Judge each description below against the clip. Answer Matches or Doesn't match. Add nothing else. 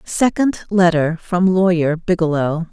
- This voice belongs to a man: Doesn't match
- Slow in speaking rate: Matches